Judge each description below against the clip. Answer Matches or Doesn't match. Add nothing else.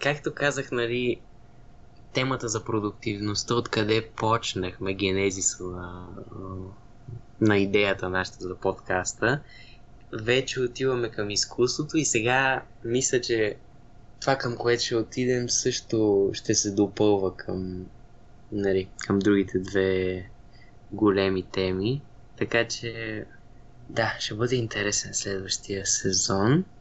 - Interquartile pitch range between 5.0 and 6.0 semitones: Doesn't match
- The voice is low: Matches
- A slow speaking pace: Matches